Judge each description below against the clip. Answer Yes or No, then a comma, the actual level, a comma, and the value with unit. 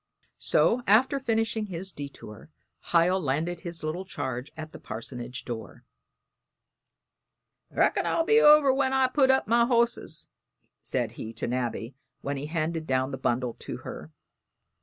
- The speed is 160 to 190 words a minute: No, average, 145 wpm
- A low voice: No, medium, 165 Hz